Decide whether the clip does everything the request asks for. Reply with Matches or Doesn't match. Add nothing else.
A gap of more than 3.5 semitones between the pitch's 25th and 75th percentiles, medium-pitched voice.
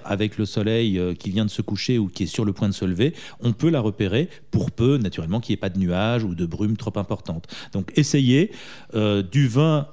Doesn't match